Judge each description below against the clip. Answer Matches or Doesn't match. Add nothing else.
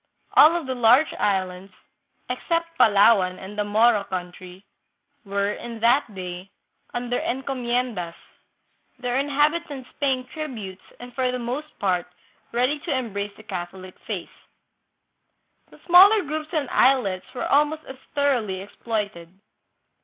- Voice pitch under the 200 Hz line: Doesn't match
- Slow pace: Matches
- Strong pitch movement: Matches